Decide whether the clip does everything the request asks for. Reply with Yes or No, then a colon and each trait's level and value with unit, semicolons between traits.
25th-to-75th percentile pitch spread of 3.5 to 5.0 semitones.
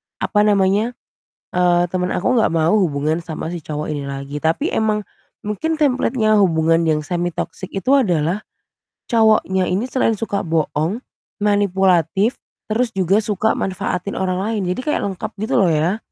Yes: average, 4.6 semitones